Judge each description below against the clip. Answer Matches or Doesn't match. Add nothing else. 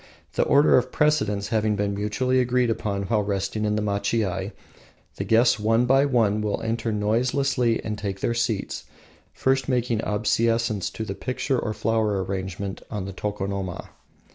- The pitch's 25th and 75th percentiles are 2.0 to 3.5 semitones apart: Matches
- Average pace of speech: Matches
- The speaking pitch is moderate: Doesn't match